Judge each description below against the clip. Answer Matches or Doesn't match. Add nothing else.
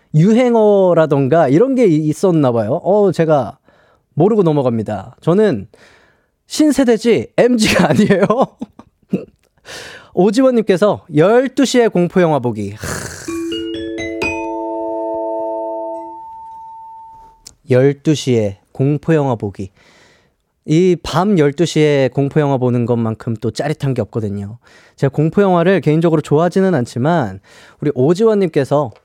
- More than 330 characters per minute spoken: Doesn't match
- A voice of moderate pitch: Matches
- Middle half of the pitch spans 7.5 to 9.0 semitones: Matches